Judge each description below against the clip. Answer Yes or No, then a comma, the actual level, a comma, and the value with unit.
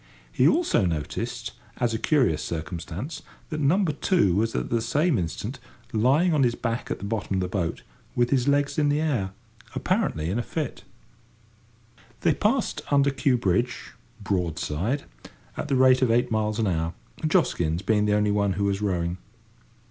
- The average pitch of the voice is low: Yes, low, 115 Hz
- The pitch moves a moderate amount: No, wide, 6.7 semitones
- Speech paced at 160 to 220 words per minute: Yes, average, 170 wpm